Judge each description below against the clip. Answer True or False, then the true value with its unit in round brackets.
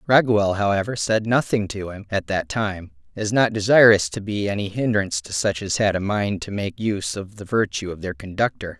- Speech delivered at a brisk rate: True (210 wpm)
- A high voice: False (105 Hz)